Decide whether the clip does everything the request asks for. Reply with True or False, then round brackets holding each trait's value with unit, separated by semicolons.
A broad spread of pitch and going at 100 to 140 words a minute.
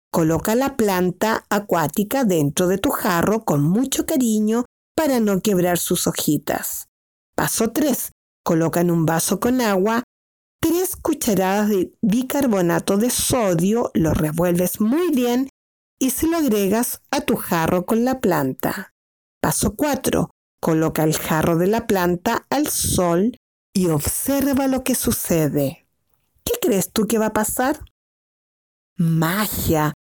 True (6.5 semitones; 135 wpm)